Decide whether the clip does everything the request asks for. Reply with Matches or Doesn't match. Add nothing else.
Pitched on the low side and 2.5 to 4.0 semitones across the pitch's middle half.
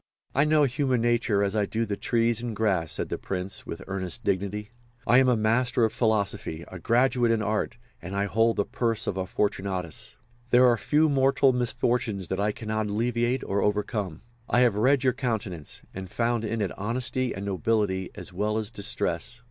Matches